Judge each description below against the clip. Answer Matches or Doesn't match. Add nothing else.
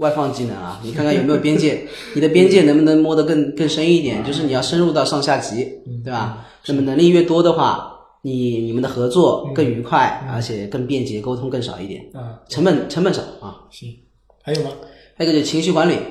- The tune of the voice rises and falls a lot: Doesn't match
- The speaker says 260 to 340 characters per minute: Matches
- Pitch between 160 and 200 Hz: Doesn't match